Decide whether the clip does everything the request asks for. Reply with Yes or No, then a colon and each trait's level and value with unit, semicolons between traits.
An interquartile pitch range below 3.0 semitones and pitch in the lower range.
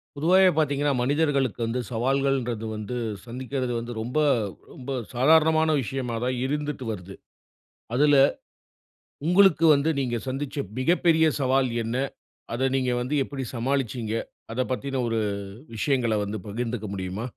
No: average, 3.5 semitones; low, 130 Hz